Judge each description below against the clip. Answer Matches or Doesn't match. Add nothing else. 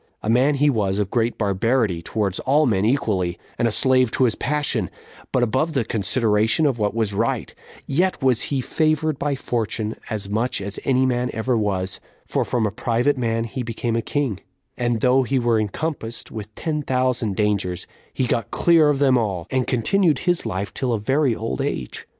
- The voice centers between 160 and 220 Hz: Doesn't match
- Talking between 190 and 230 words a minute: Matches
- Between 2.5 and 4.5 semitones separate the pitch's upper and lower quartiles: Matches